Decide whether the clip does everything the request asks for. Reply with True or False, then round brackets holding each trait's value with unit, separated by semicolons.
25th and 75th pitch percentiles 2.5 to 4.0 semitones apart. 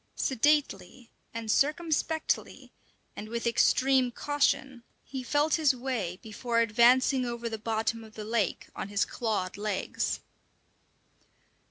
True (3.5 semitones)